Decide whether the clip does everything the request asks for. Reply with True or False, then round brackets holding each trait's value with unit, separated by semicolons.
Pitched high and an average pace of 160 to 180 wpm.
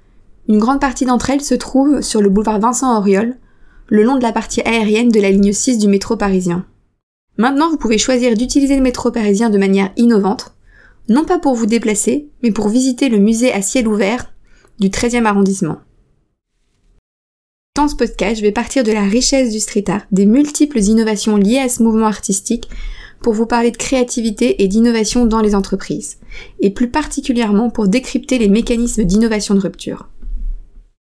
True (225 Hz; 175 wpm)